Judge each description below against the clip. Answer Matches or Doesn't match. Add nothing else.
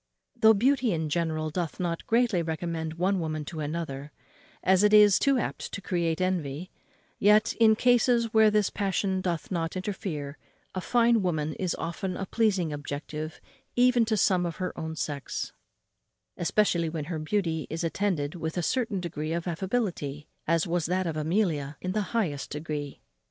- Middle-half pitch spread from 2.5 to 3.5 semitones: Doesn't match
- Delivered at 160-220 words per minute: Matches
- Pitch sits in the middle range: Matches